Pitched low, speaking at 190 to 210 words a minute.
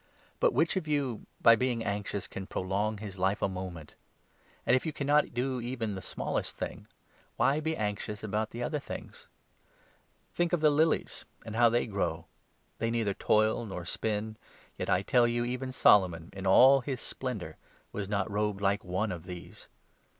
No: low, 110 Hz; average, 180 wpm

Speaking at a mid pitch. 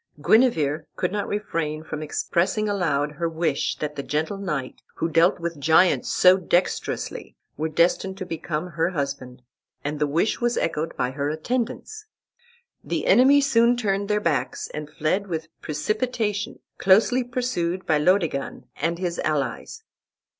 Yes: medium, 170 Hz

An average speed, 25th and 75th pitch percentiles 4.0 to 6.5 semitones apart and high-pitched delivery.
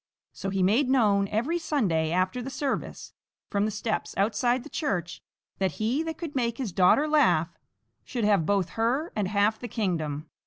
Yes: average, 180 wpm; wide, 5.5 semitones; high, 215 Hz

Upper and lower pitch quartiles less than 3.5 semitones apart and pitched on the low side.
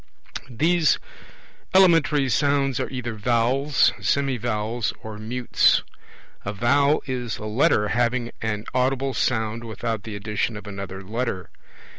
No: average, 4.0 semitones; low, 120 Hz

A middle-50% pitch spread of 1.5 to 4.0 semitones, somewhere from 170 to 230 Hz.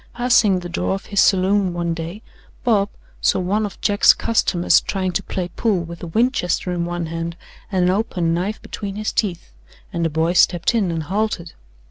Yes: average, 3.2 semitones; medium, 185 Hz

